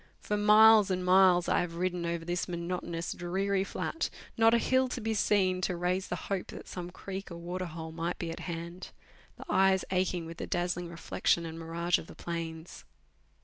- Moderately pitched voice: Yes, medium, 180 Hz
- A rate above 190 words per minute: Yes, average, 200 wpm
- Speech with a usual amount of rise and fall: No, narrow, 2.1 semitones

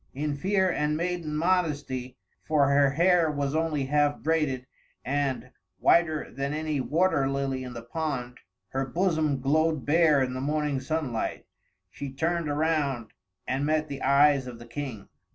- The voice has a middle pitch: Yes, medium, 145 Hz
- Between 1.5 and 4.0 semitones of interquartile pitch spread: Yes, average, 2.8 semitones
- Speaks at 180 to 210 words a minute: No, average, 150 wpm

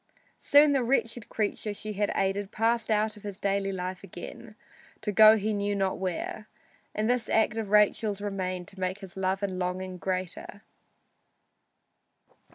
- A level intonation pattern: Yes, narrow, 2.3 semitones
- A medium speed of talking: Yes, average, 160 wpm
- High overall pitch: Yes, high, 205 Hz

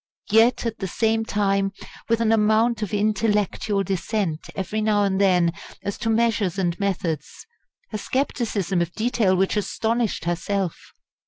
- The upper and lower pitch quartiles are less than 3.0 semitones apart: Yes, narrow, 2.6 semitones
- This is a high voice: Yes, high, 205 Hz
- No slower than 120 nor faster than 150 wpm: Yes, average, 145 wpm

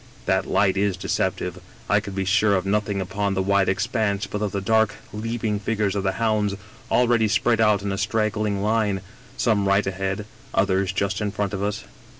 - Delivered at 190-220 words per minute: Yes, average, 195 wpm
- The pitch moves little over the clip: Yes, narrow, 1.6 semitones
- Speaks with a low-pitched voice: Yes, low, 100 Hz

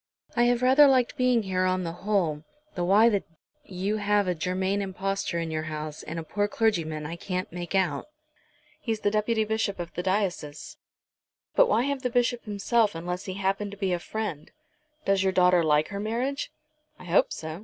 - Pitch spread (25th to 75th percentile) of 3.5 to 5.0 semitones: Yes, average, 3.9 semitones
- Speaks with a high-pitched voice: Yes, high, 195 Hz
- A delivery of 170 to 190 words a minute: No, average, 200 wpm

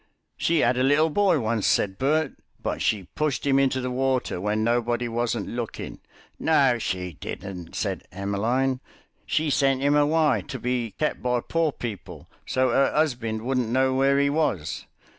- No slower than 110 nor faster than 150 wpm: No, average, 165 wpm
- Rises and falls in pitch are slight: No, average, 3.8 semitones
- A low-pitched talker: Yes, low, 125 Hz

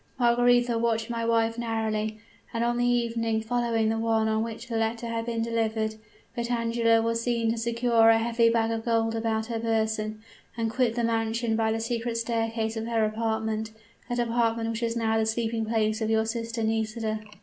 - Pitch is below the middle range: No, high, 230 Hz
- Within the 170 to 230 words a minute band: Yes, average, 190 wpm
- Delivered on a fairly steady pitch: Yes, narrow, 0.9 semitones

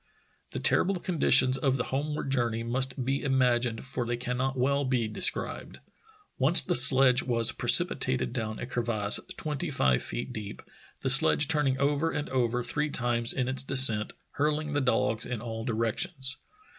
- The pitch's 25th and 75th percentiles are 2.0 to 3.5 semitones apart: Yes, average, 2.9 semitones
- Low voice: Yes, low, 130 Hz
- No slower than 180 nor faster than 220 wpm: No, average, 165 wpm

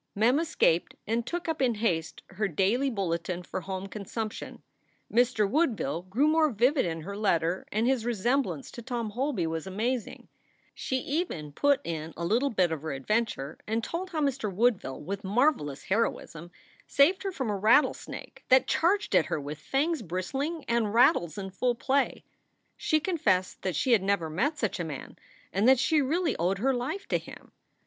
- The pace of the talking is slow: No, average, 180 wpm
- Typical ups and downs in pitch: No, wide, 6.7 semitones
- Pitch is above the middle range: Yes, high, 225 Hz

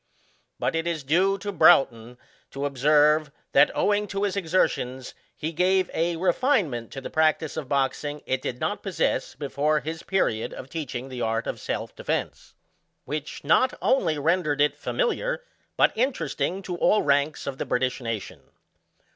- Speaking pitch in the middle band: Yes, medium, 155 Hz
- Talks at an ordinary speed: Yes, average, 160 wpm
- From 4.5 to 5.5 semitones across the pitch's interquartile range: Yes, average, 4.9 semitones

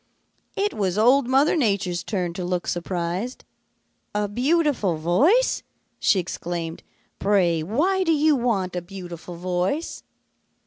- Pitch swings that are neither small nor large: No, wide, 7.4 semitones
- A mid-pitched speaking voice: No, high, 195 Hz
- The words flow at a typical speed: No, slow, 125 wpm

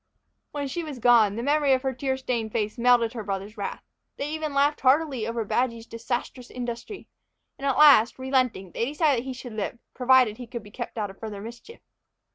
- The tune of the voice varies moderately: Yes, average, 3.3 semitones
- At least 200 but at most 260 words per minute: Yes, fast, 205 wpm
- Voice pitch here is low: No, high, 245 Hz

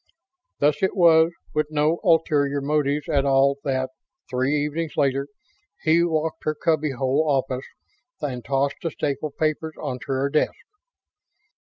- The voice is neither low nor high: Yes, medium, 145 Hz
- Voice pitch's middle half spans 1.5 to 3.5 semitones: Yes, narrow, 2.4 semitones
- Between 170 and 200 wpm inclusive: No, average, 140 wpm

